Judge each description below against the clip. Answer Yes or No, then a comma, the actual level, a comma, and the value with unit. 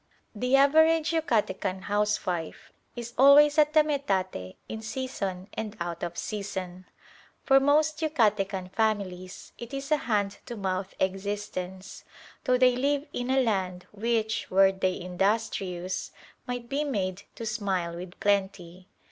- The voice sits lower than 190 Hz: No, high, 205 Hz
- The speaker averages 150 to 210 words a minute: No, slow, 135 wpm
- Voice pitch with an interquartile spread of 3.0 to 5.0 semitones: No, wide, 5.4 semitones